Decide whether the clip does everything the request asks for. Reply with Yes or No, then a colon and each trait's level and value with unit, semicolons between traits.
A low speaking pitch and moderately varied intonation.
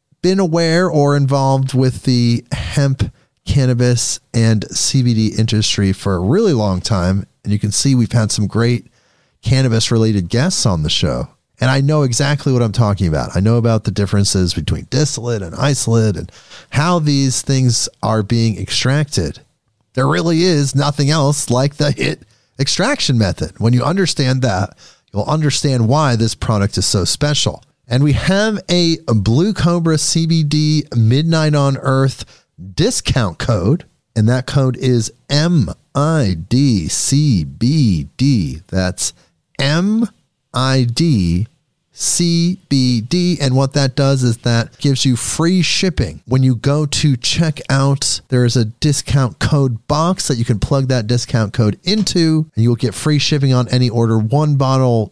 Yes: low, 130 Hz; average, 4.6 semitones